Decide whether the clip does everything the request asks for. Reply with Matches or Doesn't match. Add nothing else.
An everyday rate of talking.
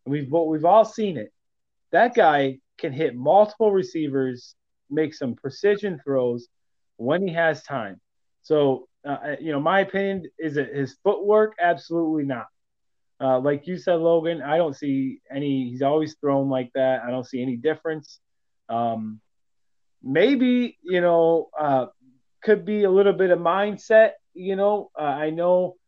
Matches